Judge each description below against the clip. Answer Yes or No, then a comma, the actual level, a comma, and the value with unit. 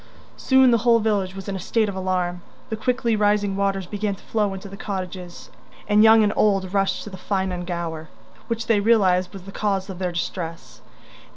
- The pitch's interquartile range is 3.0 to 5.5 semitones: No, narrow, 2.4 semitones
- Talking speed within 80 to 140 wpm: No, average, 195 wpm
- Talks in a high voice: Yes, high, 195 Hz